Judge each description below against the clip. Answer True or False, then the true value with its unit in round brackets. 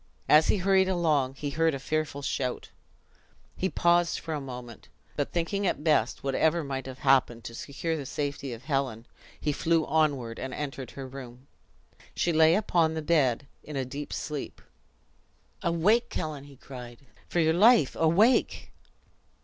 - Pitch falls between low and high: True (150 Hz)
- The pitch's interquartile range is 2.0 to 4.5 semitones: True (3.8 semitones)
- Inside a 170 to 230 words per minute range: False (160 wpm)